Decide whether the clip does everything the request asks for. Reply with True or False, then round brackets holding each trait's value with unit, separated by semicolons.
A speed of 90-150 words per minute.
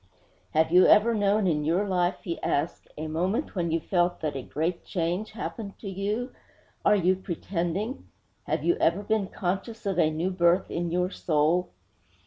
False (175 wpm)